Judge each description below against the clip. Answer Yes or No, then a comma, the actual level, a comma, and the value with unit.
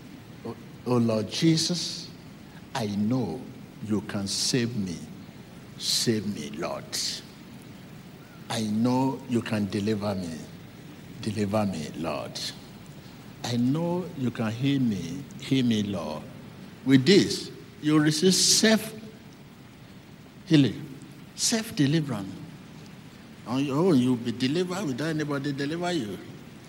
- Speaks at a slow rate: Yes, slow, 105 wpm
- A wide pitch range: Yes, wide, 6.7 semitones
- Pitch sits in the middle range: No, low, 130 Hz